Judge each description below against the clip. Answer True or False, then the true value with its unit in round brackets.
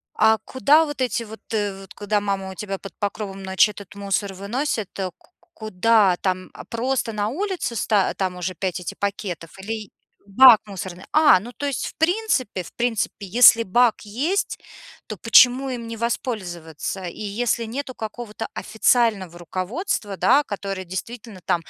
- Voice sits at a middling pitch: False (210 Hz)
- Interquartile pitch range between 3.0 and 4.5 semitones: True (4.0 semitones)